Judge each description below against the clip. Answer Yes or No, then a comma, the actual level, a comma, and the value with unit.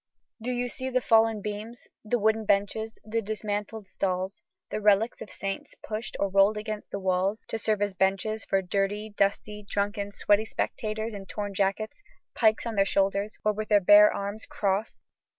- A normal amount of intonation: No, narrow, 1.7 semitones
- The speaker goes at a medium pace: Yes, average, 175 wpm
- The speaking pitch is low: No, high, 210 Hz